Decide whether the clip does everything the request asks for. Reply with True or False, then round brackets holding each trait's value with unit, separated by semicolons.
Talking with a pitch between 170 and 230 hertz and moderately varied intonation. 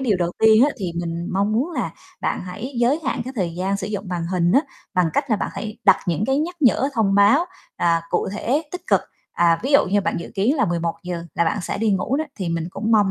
False (200 Hz; 5.7 semitones)